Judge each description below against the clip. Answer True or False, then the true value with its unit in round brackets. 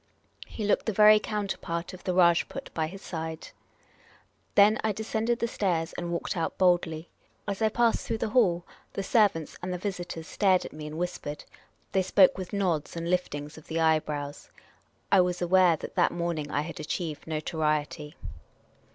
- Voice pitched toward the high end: False (175 Hz)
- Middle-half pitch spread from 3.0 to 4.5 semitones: True (3.7 semitones)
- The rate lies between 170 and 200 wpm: True (175 wpm)